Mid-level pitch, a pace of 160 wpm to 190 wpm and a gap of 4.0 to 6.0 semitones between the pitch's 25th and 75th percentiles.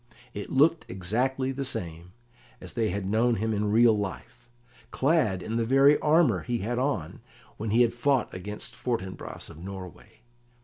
No: low, 115 Hz; average, 165 wpm; average, 5.0 semitones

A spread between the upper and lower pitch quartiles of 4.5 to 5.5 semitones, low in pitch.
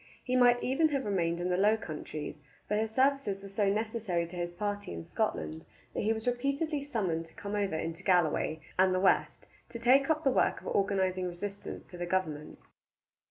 No: average, 5.2 semitones; high, 200 Hz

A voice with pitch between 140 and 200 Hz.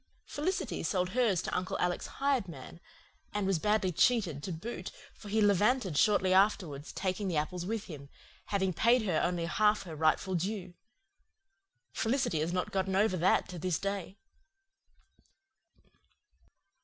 Yes: high, 190 Hz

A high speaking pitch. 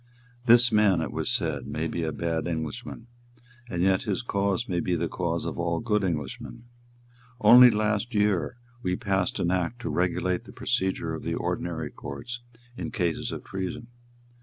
No: very low, 95 Hz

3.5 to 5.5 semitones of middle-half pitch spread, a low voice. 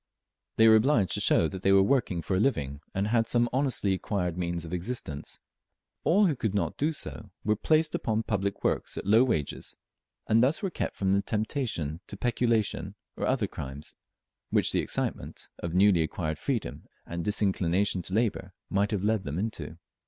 Yes: average, 4.6 semitones; low, 100 Hz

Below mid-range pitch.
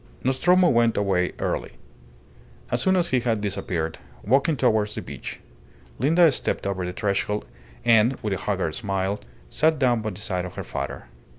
Yes: low, 110 Hz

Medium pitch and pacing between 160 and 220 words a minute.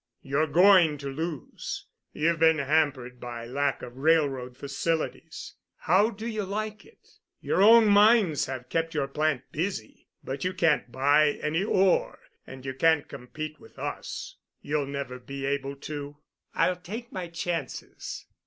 No: medium, 155 Hz; average, 150 wpm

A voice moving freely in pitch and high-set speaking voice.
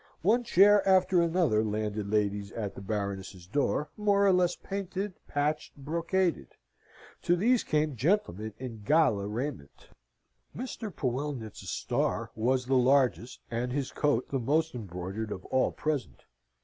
No: wide, 8.2 semitones; low, 135 Hz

